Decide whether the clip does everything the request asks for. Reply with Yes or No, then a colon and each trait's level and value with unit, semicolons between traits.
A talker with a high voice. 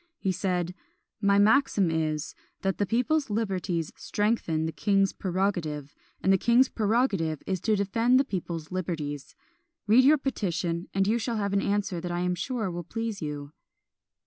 Yes: high, 195 Hz